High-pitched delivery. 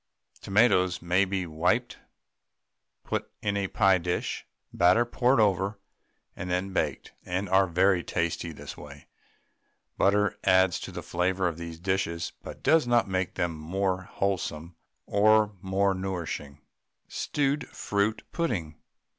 No: very low, 95 Hz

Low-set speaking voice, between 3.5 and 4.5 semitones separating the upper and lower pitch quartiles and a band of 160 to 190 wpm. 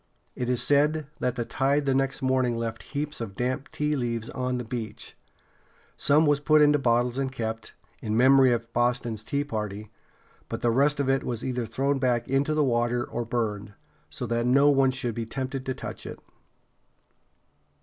No: low, 125 Hz; average, 2.7 semitones; average, 185 wpm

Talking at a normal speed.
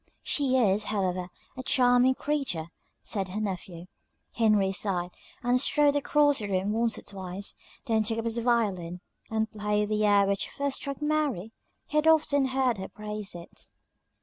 Yes: average, 165 wpm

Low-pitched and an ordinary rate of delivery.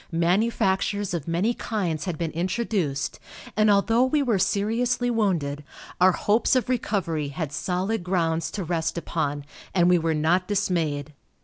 No: medium, 180 Hz; average, 145 wpm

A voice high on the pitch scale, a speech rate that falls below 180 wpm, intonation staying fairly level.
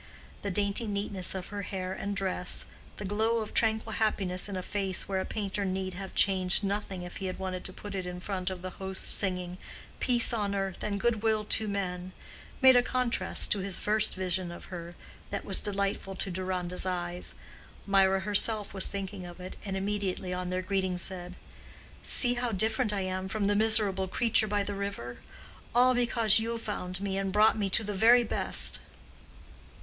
No: high, 195 Hz; average, 190 wpm; narrow, 2.3 semitones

